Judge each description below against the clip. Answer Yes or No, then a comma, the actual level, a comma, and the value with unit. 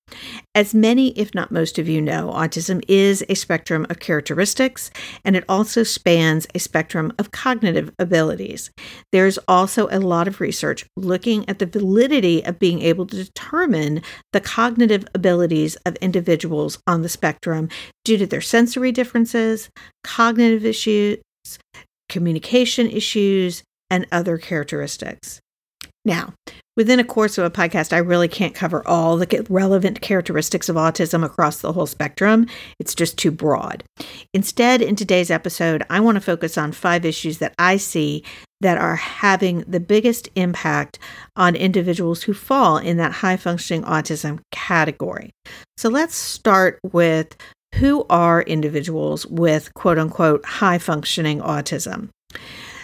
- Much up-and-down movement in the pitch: No, average, 4.2 semitones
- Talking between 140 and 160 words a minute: Yes, average, 145 wpm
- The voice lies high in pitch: No, medium, 180 Hz